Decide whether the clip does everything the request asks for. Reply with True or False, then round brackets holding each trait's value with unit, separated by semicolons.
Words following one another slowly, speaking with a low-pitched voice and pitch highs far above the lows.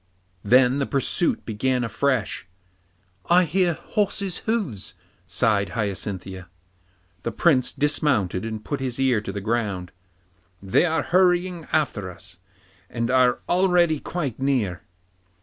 True (120 wpm; 125 Hz; 7.8 semitones)